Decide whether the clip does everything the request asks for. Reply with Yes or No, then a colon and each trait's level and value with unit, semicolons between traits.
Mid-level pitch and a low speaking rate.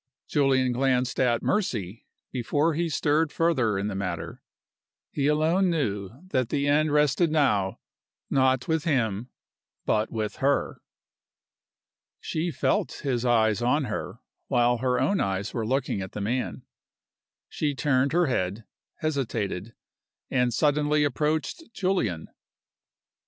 No: low, 130 Hz; slow, 125 wpm